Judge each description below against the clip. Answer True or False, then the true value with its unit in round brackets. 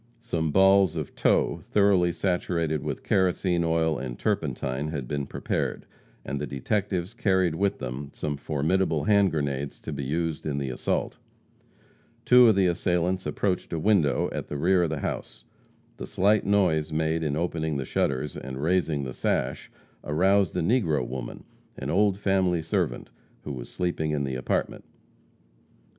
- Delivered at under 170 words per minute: True (160 wpm)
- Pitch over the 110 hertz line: False (80 Hz)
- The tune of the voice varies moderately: True (4.6 semitones)